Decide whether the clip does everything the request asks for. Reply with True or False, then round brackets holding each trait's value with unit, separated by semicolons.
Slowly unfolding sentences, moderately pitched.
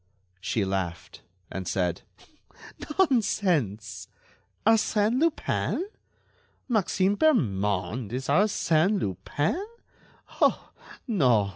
True (75 wpm; 145 Hz)